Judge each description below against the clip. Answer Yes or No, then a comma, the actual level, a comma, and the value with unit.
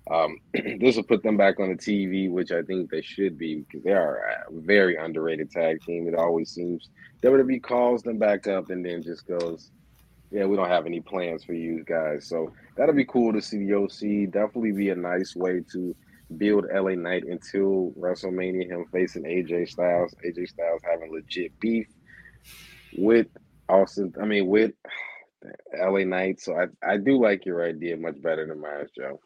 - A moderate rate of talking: Yes, average, 185 wpm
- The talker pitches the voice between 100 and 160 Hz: No, very low, 90 Hz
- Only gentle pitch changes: No, average, 3.2 semitones